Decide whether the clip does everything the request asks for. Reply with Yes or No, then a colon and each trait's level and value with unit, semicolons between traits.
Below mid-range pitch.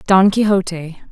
No: high, 190 Hz